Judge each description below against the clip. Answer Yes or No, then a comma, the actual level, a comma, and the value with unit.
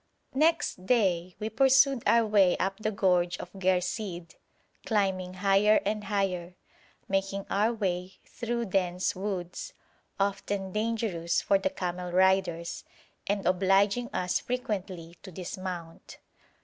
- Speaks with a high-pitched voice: Yes, high, 195 Hz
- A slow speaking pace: Yes, slow, 120 wpm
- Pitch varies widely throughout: No, average, 2.7 semitones